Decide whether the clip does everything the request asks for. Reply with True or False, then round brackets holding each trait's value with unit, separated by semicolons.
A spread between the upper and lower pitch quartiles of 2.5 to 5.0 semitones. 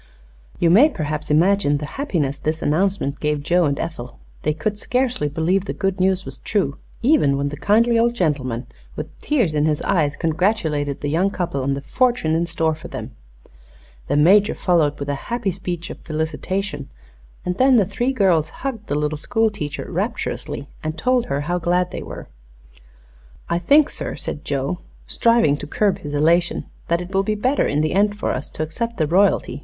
False (5.5 semitones)